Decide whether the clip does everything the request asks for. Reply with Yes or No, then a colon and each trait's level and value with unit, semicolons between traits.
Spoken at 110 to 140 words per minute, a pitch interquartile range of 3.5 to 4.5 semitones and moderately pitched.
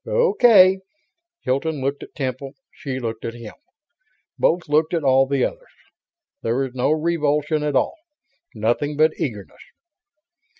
Yes: slow, 135 wpm; average, 3.8 semitones; medium, 145 Hz